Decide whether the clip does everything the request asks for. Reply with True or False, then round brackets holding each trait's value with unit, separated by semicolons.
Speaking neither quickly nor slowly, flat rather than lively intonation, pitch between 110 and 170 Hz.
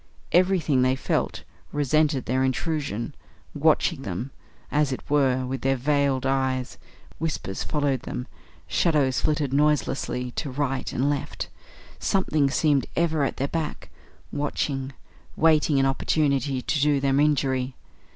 False (125 wpm; 2.3 semitones; 140 Hz)